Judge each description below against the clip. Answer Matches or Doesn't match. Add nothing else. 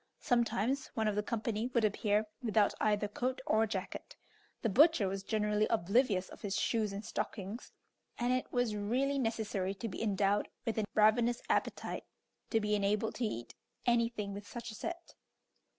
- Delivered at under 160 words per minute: Doesn't match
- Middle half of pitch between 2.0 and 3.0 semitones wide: Matches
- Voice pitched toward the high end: Matches